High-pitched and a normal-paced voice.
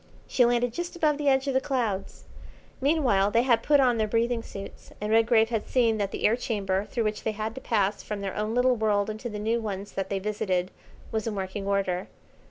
No: high, 220 Hz; fast, 225 wpm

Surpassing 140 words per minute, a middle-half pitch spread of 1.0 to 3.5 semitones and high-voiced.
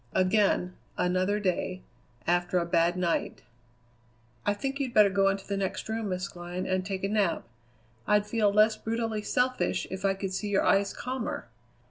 Yes: average, 170 wpm; narrow, 2.6 semitones; high, 195 Hz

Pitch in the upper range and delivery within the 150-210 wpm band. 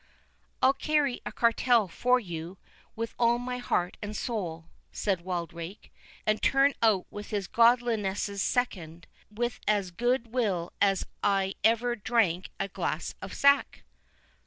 No: high, 215 Hz; slow, 135 wpm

